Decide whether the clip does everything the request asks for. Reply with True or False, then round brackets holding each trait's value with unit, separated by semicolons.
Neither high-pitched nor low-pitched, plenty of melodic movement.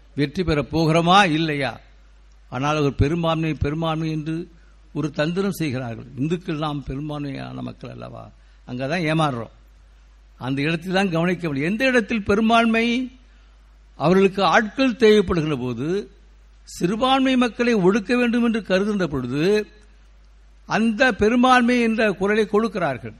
True (160 Hz; 8.3 semitones)